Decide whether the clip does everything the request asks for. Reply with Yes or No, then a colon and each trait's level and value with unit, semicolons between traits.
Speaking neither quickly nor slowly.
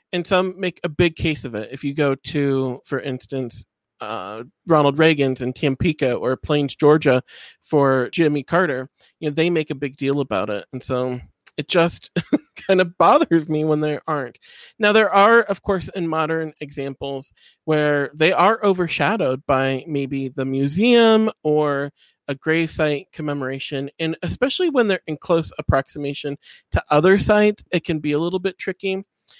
Yes: average, 170 wpm